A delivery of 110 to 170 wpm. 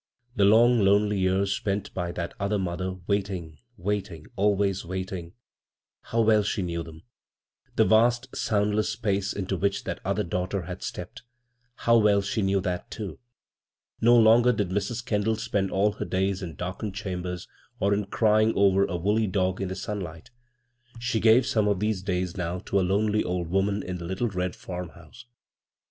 No: average, 185 wpm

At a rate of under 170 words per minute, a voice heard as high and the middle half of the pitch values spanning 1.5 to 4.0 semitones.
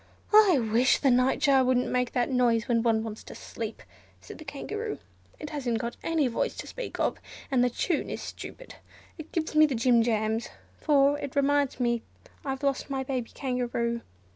No: average, 185 wpm; very high, 255 Hz; average, 3.3 semitones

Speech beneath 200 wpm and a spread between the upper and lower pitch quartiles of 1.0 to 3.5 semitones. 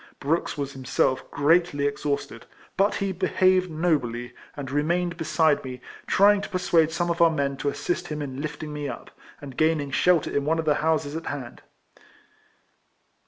Yes: average, 165 wpm; average, 3.2 semitones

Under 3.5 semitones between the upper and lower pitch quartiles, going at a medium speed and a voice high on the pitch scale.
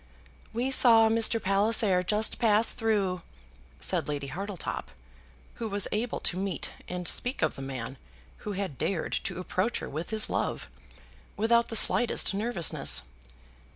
No: average, 3.8 semitones; average, 145 wpm; high, 205 Hz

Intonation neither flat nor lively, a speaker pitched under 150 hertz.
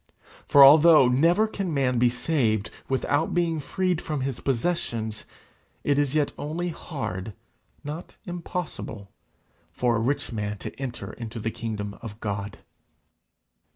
No: wide, 6.2 semitones; low, 135 Hz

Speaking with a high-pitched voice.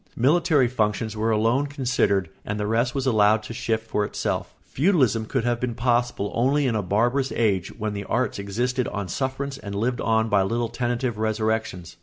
No: low, 115 Hz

